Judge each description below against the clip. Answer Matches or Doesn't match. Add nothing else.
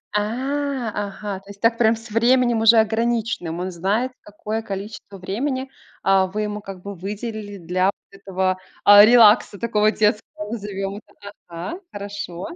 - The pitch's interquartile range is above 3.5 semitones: Doesn't match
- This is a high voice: Matches